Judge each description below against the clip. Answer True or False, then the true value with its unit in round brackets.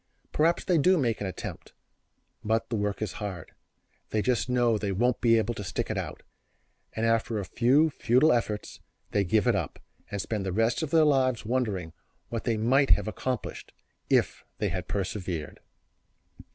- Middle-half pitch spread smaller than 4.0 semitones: True (3.6 semitones)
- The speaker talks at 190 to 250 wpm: False (180 wpm)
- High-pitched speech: False (115 Hz)